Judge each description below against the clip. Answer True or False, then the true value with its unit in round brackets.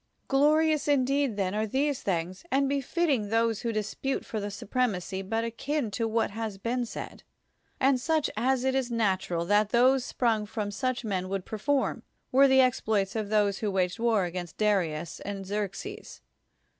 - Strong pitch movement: False (4.7 semitones)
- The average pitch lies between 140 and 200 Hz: False (225 Hz)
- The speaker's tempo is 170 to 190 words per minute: True (180 wpm)